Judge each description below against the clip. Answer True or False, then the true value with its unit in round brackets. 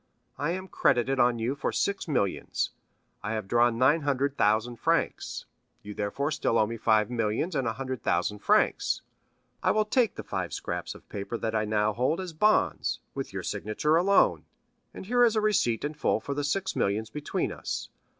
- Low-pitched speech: True (130 Hz)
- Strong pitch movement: True (6.5 semitones)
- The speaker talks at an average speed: True (190 wpm)